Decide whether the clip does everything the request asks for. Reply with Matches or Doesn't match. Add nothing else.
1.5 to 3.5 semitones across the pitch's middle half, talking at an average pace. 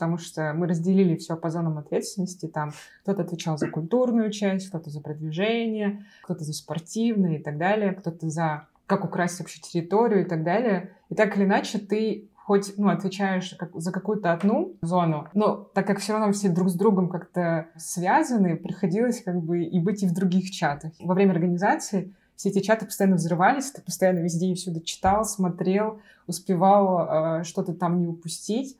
Doesn't match